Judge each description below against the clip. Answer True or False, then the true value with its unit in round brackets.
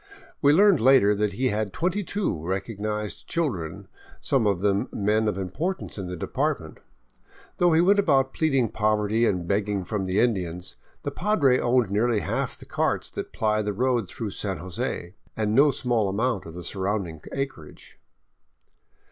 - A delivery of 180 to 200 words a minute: False (165 wpm)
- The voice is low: True (105 Hz)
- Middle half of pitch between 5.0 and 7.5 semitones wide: True (5.3 semitones)